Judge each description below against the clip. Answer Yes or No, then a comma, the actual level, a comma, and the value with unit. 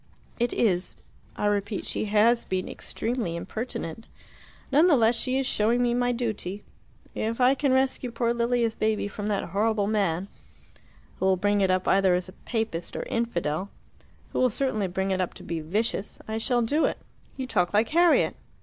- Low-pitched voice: No, high, 220 Hz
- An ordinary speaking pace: Yes, average, 180 wpm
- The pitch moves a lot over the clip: No, average, 4.0 semitones